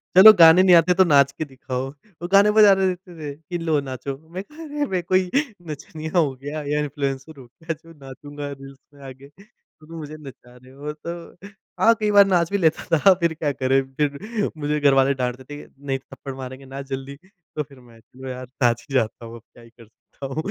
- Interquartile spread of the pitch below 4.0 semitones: No, average, 4.3 semitones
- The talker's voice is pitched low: No, medium, 145 Hz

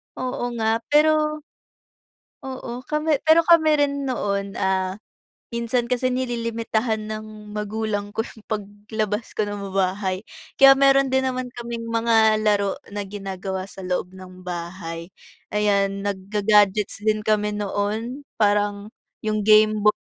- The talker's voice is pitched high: Yes, high, 215 Hz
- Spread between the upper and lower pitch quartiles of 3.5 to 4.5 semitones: No, average, 2.9 semitones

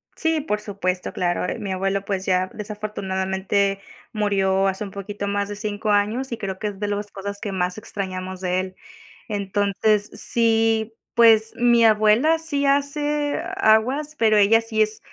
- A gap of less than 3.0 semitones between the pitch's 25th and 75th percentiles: Yes, narrow, 2.5 semitones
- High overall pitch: Yes, high, 205 Hz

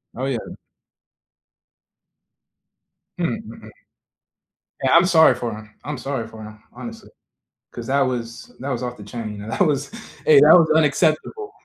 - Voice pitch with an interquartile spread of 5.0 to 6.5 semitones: Yes, wide, 5.6 semitones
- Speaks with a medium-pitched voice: No, low, 130 Hz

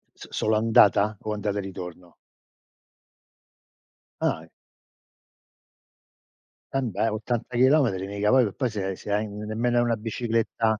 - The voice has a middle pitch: No, low, 110 Hz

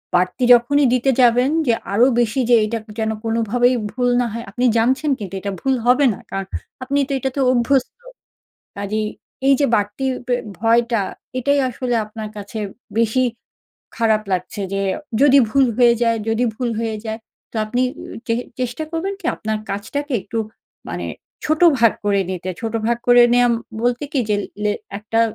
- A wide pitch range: No, average, 2.9 semitones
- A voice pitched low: No, high, 235 Hz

